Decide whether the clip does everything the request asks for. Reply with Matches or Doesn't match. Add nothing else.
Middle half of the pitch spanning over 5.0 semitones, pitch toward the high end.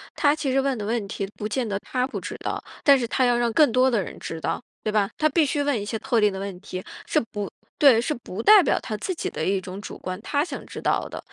Matches